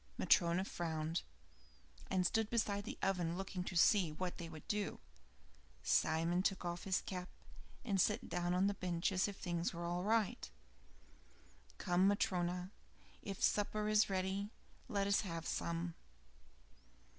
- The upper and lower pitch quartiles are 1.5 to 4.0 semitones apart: Yes, narrow, 2.6 semitones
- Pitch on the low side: No, medium, 185 Hz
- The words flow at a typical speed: Yes, average, 145 wpm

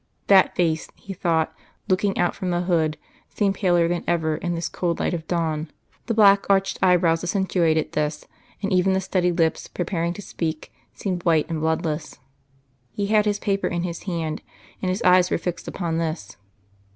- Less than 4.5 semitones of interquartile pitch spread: Yes, average, 2.7 semitones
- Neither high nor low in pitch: Yes, medium, 175 Hz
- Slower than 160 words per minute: No, average, 180 wpm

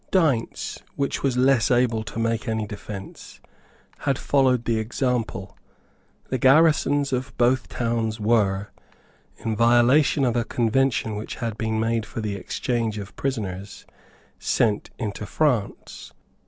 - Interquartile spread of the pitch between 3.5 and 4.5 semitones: No, average, 3.1 semitones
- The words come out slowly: Yes, slow, 130 wpm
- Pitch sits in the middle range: No, low, 115 Hz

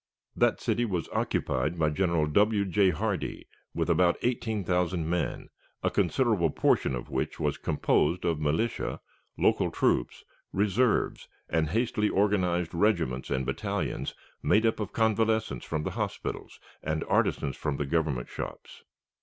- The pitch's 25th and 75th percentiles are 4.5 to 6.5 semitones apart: Yes, average, 5.2 semitones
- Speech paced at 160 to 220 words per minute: No, average, 140 wpm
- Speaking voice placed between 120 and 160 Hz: No, very low, 90 Hz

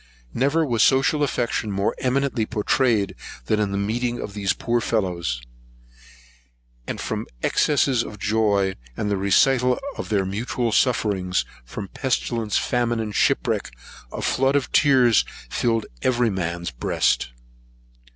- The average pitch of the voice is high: No, low, 115 Hz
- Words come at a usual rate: No, slow, 130 wpm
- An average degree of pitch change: Yes, average, 4.1 semitones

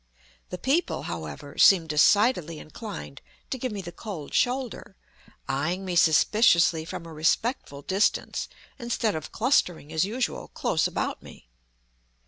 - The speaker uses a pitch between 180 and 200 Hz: Yes, medium, 185 Hz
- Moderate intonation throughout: No, wide, 6.3 semitones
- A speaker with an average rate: No, slow, 130 wpm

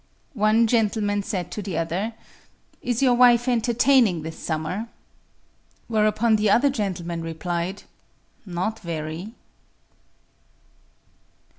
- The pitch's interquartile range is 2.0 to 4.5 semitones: No, average, 5.0 semitones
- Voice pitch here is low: No, high, 210 Hz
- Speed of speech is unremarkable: No, slow, 100 wpm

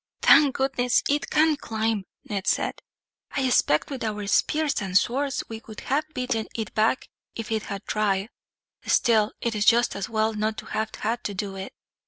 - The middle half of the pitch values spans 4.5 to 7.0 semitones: No, average, 3.3 semitones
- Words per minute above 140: Yes, average, 185 wpm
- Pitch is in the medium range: No, high, 220 Hz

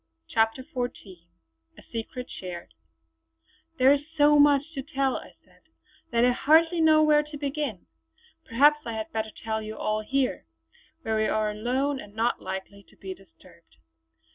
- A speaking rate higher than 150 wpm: Yes, average, 160 wpm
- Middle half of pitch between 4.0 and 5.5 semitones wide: Yes, average, 5.0 semitones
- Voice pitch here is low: No, high, 245 Hz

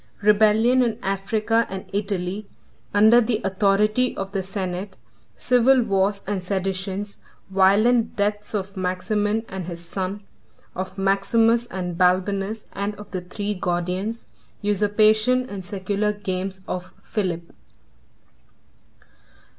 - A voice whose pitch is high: Yes, high, 200 Hz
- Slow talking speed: Yes, slow, 105 wpm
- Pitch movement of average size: No, narrow, 2.2 semitones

